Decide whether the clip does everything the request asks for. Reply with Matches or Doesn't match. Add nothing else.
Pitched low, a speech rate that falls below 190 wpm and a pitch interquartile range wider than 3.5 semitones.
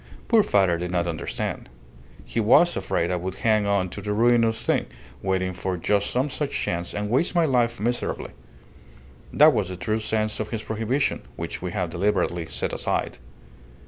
Matches